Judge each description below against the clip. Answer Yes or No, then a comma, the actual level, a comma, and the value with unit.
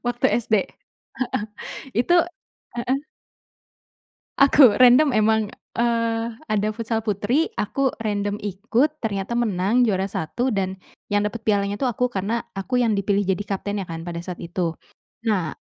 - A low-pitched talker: No, high, 215 Hz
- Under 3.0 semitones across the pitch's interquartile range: No, average, 3.3 semitones